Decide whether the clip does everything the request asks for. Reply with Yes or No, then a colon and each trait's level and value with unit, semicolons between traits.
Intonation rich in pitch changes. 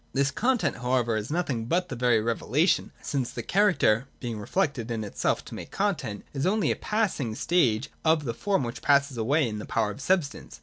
Yes: wide, 7.0 semitones